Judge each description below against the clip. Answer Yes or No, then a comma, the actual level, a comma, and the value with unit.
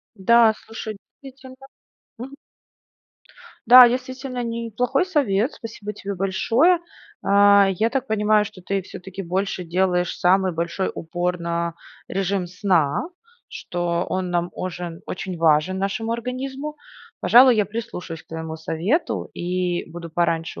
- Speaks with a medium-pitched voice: No, high, 195 Hz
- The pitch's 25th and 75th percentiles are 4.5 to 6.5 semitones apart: Yes, average, 4.9 semitones